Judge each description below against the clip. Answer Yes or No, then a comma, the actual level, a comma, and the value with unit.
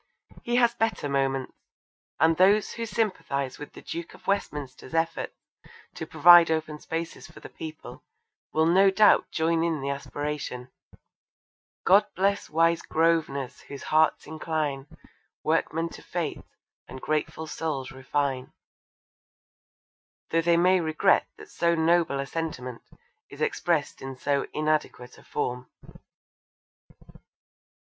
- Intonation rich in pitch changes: No, average, 3.4 semitones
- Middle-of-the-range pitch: Yes, medium, 160 Hz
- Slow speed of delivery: Yes, slow, 125 wpm